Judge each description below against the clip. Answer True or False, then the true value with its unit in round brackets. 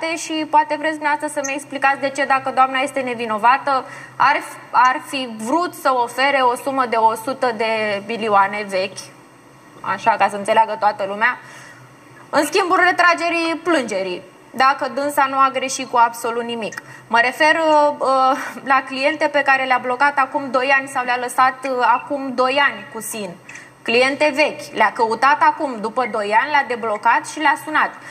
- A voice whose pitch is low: False (265 Hz)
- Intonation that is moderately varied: True (3.8 semitones)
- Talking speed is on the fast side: False (160 wpm)